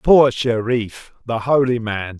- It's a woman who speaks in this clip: No, male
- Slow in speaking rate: Yes, slow, 110 wpm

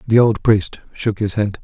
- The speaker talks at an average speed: No, fast, 220 wpm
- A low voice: Yes, low, 105 Hz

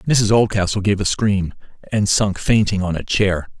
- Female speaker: No, male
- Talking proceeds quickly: No, average, 185 wpm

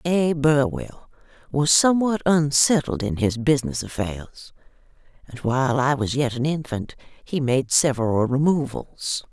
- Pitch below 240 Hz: Yes, low, 135 Hz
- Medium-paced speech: No, slow, 130 wpm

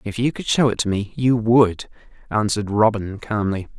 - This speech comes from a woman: No, male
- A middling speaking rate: Yes, average, 190 wpm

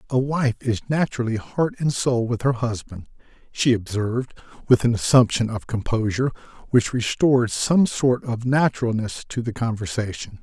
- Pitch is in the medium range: No, low, 120 Hz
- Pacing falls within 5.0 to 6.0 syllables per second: Yes, 5.1 syllables/s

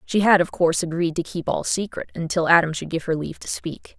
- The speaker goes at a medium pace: No, fast, 255 wpm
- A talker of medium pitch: Yes, medium, 170 Hz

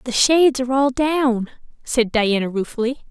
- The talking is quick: No, average, 155 wpm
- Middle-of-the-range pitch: No, very high, 250 Hz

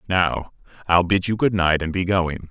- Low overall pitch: Yes, very low, 90 Hz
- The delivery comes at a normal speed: Yes, average, 190 wpm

